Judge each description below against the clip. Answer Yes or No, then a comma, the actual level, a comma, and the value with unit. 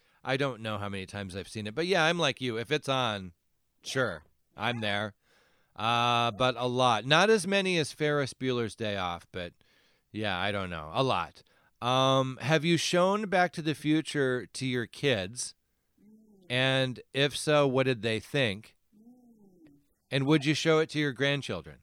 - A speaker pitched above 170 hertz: No, low, 130 Hz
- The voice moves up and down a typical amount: No, wide, 5.7 semitones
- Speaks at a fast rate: No, average, 180 wpm